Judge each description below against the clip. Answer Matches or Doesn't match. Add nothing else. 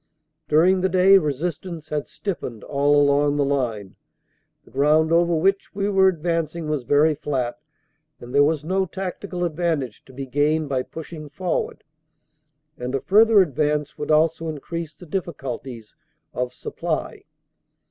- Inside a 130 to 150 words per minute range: Matches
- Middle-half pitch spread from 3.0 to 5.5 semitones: Matches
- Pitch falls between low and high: Matches